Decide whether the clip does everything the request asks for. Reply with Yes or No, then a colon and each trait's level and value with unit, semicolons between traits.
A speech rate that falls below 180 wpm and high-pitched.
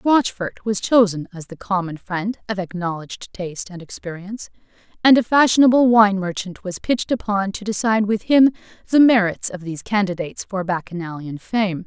Yes: average, 160 wpm; high, 200 Hz